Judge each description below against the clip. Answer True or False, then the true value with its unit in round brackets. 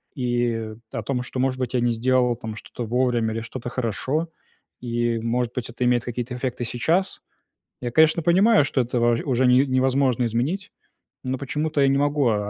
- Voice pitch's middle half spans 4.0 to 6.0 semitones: False (2.4 semitones)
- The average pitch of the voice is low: True (125 Hz)